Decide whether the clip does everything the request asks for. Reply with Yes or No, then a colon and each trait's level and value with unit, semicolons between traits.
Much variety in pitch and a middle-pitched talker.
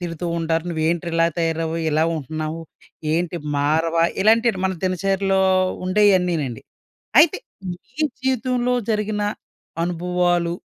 No: average, 3.2 semitones; medium, 175 Hz